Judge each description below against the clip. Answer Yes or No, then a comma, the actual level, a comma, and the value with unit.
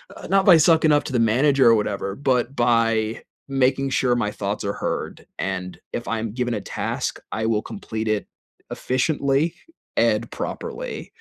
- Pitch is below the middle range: Yes, low, 120 Hz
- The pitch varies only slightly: No, average, 4.1 semitones